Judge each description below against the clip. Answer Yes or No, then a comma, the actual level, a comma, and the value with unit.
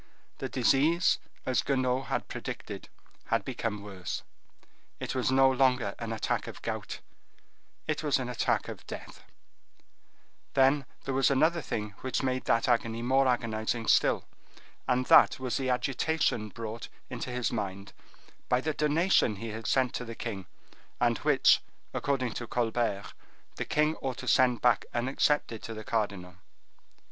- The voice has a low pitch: Yes, low, 125 Hz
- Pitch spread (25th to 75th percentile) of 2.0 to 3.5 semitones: Yes, average, 3.0 semitones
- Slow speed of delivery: No, average, 150 wpm